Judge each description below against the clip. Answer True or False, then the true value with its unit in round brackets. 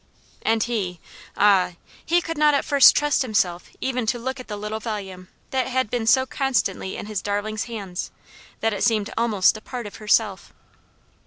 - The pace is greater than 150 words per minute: True (180 wpm)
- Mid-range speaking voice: False (220 Hz)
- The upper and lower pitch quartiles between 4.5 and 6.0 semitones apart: False (3.9 semitones)